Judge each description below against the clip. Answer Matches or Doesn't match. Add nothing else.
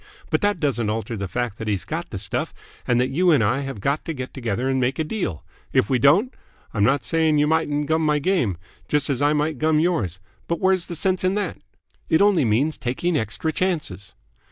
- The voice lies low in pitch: Doesn't match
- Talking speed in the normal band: Doesn't match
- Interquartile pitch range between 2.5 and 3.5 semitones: Doesn't match